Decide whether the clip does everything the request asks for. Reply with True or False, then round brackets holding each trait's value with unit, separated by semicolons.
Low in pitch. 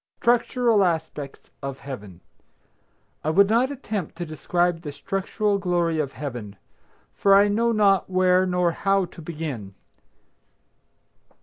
False (180 Hz)